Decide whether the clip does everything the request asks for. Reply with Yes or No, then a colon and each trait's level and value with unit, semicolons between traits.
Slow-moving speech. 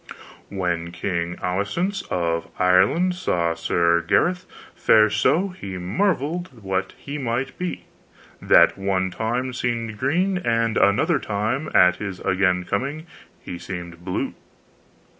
Yes: slow, 120 wpm